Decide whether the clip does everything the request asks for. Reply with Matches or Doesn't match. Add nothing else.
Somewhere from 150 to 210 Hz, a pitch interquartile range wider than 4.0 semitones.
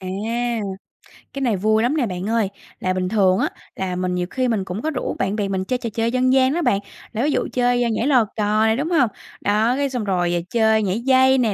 Doesn't match